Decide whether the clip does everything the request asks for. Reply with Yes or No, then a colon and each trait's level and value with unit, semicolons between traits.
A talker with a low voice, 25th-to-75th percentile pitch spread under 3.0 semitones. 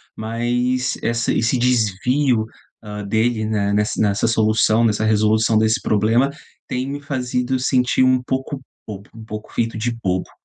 Yes: low, 115 Hz; narrow, 2.5 semitones